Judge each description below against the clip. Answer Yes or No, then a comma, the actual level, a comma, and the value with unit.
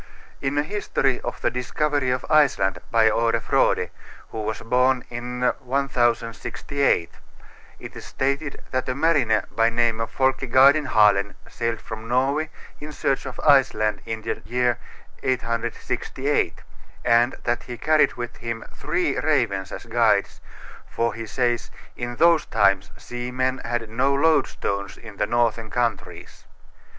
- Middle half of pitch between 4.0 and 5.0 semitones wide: No, average, 2.9 semitones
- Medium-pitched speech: No, low, 120 Hz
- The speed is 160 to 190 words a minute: No, average, 140 wpm